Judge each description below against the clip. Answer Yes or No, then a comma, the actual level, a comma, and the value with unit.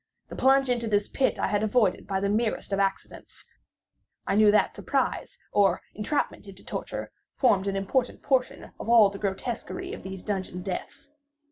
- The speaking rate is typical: Yes, average, 170 wpm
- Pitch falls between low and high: No, high, 210 Hz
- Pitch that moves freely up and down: No, average, 4.1 semitones